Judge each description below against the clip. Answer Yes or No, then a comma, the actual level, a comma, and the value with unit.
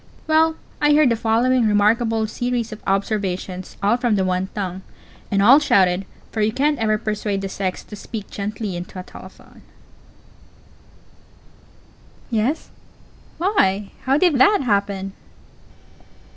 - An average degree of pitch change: Yes, average, 4.1 semitones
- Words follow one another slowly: Yes, slow, 130 wpm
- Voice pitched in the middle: No, high, 215 Hz